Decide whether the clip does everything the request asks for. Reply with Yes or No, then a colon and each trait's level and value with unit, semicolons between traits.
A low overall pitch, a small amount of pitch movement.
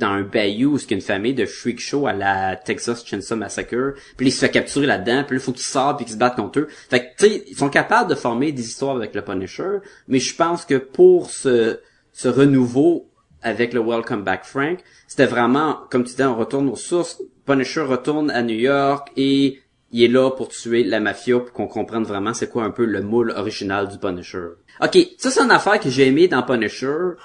No: low, 125 Hz; average, 3.4 semitones